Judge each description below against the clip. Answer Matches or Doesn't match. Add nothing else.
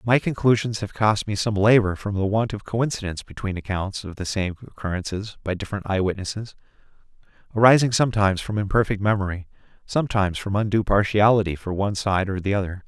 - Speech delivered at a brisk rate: Doesn't match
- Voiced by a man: Matches